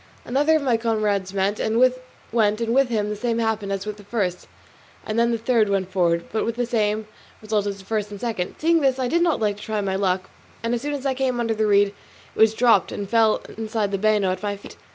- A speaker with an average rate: No, fast, 250 wpm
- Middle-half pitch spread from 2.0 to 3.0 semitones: Yes, average, 2.7 semitones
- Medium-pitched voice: No, high, 215 Hz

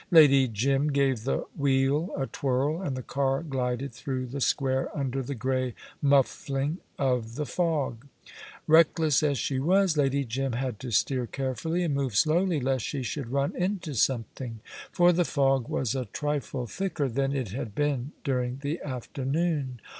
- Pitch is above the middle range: No, low, 135 Hz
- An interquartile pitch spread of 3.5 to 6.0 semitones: No, narrow, 2.5 semitones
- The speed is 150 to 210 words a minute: Yes, average, 160 wpm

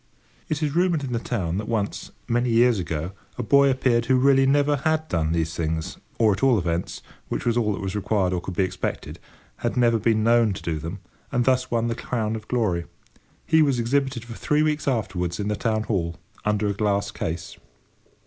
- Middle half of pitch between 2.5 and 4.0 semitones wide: No, average, 5.2 semitones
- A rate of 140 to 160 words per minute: No, fast, 205 wpm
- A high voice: No, low, 115 Hz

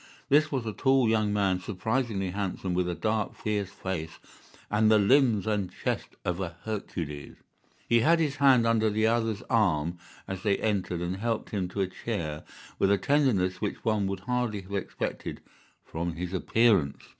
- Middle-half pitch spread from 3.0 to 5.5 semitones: Yes, average, 3.7 semitones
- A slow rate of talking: No, average, 175 wpm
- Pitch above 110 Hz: No, low, 105 Hz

